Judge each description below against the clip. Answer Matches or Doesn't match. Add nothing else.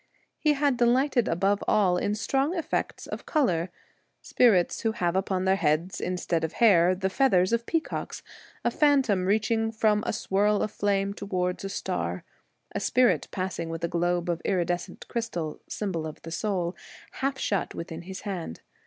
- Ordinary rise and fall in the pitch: Matches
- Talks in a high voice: Matches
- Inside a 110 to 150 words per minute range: Doesn't match